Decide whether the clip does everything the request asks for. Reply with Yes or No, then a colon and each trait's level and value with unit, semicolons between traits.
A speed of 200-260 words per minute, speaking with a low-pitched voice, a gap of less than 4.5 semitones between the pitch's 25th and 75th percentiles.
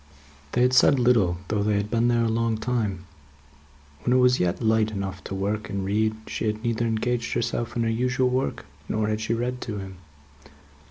Yes: fast, 205 wpm; low, 110 Hz; narrow, 2.6 semitones